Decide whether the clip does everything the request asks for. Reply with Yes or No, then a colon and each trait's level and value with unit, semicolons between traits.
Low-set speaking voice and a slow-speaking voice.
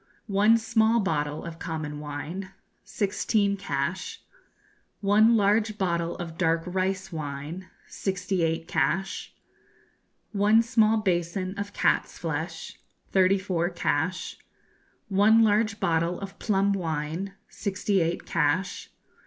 No: high, 190 Hz; slow, 110 wpm